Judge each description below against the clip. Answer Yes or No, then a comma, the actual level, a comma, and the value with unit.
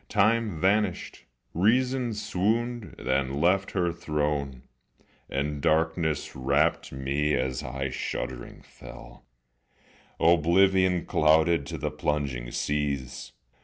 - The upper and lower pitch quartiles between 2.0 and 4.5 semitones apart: No, wide, 5.6 semitones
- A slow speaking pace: Yes, slow, 95 wpm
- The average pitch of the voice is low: Yes, very low, 80 Hz